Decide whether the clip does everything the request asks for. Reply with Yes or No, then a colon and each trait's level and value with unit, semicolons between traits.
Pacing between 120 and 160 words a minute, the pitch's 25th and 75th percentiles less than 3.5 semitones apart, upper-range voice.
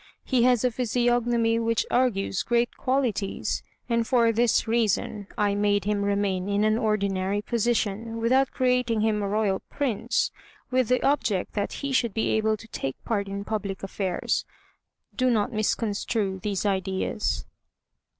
Yes: average, 150 wpm; average, 2.9 semitones; high, 220 Hz